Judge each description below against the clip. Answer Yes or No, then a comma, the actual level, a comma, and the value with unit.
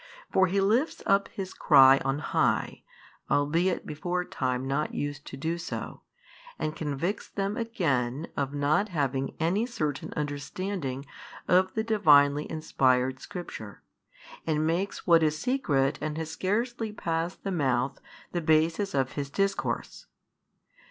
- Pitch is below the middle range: No, medium, 160 Hz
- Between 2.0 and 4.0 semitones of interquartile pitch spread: No, average, 5.2 semitones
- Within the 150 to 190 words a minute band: No, average, 140 wpm